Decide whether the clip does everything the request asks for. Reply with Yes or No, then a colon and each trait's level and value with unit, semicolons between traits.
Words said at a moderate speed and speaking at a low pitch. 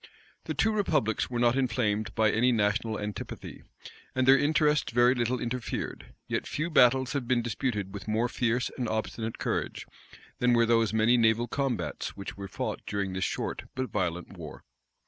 Yes: average, 170 wpm; low, 120 Hz